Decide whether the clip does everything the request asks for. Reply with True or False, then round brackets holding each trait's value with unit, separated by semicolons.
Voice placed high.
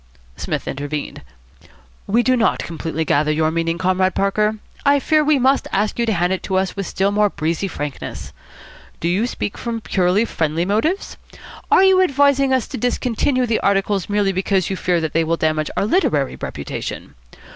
True (195 Hz)